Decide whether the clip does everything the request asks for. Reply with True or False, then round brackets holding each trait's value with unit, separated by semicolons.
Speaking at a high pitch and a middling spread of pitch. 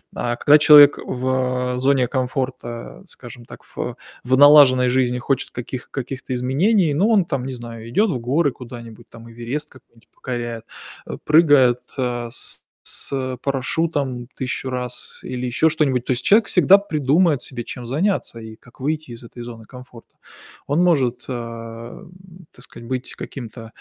False (130 Hz; 3.3 semitones)